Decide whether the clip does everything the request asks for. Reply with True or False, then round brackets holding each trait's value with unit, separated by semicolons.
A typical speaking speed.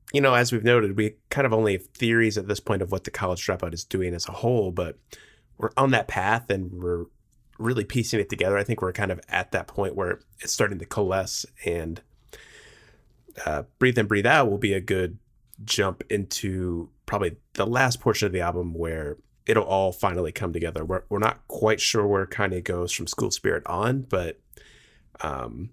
False (210 wpm)